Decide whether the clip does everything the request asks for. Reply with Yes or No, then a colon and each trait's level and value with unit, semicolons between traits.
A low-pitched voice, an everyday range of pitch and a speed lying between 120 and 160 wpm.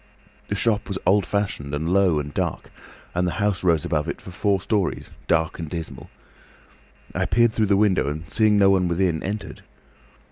No: very low, 95 Hz; average, 3.7 semitones; average, 185 wpm